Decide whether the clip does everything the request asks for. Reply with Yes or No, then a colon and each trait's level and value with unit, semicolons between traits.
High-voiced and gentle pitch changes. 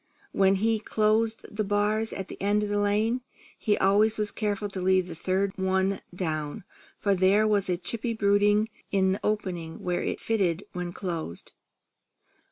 Yes: high, 200 Hz; narrow, 2.2 semitones